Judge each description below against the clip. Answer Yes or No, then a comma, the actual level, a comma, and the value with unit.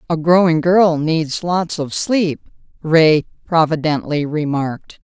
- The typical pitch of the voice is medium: Yes, medium, 160 Hz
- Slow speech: Yes, slow, 120 wpm